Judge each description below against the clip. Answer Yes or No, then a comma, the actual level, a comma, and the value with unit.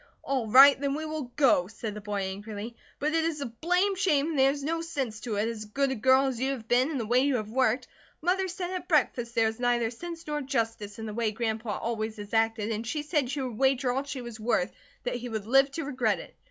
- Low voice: No, very high, 250 Hz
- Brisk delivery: Yes, fast, 260 wpm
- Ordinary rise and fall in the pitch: Yes, average, 4.3 semitones